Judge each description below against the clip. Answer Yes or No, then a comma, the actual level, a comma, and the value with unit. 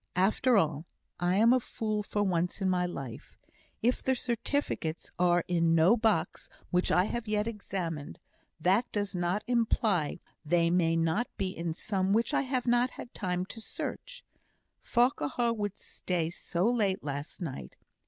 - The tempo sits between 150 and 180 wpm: Yes, average, 165 wpm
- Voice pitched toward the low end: No, high, 190 Hz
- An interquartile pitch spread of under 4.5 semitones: No, average, 5.2 semitones